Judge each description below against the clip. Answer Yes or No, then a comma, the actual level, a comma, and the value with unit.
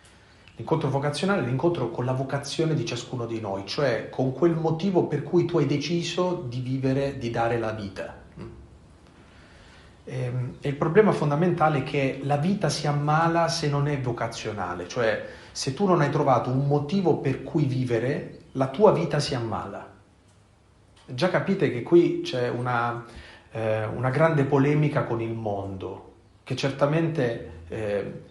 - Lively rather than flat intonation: Yes, wide, 5.7 semitones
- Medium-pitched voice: No, low, 130 Hz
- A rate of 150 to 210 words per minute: Yes, average, 155 wpm